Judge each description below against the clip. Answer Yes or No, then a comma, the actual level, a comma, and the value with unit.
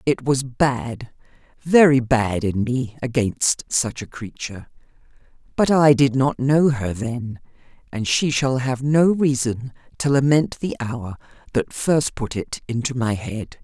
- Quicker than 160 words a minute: No, average, 155 wpm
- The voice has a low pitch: Yes, low, 130 Hz